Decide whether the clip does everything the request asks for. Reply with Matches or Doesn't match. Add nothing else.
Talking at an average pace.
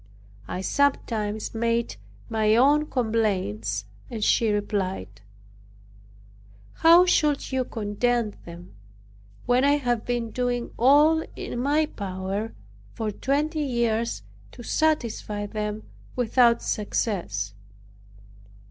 Doesn't match